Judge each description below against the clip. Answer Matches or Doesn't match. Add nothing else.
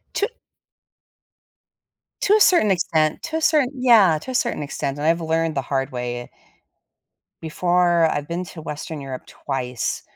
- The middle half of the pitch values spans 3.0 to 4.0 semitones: Doesn't match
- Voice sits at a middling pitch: Matches